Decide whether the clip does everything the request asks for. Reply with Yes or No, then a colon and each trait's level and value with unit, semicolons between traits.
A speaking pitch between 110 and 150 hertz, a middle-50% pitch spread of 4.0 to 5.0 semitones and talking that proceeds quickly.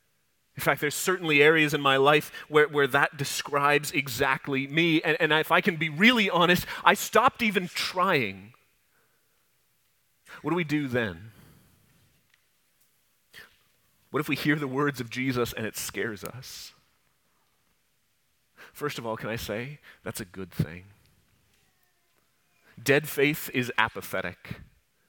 No: medium, 140 Hz; average, 4.6 semitones; slow, 135 wpm